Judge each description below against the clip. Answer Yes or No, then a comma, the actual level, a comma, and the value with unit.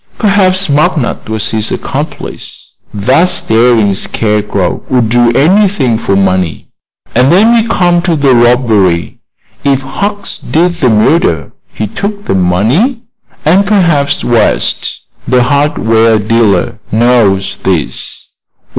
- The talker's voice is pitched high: No, low, 125 Hz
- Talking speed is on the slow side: Yes, slow, 120 wpm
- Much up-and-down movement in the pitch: Yes, wide, 8.2 semitones